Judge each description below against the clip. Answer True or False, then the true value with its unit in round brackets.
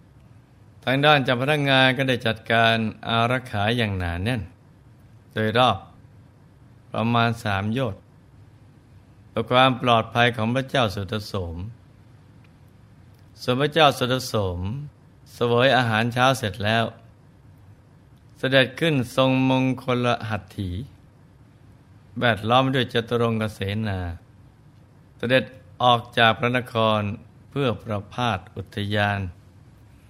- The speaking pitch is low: True (120 Hz)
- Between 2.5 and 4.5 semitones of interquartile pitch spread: True (3.1 semitones)